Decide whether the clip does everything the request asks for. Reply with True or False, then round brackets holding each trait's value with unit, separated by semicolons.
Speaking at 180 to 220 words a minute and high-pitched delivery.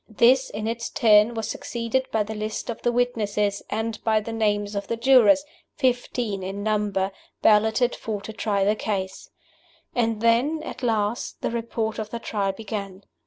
False (170 wpm; 220 Hz)